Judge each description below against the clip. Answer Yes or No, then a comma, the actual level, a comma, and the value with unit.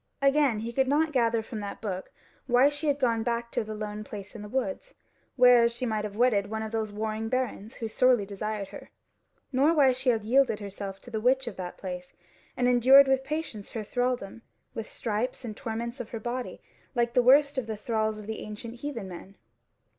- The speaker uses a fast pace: Yes, fast, 210 wpm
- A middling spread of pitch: Yes, average, 3.3 semitones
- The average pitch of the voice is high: Yes, high, 235 Hz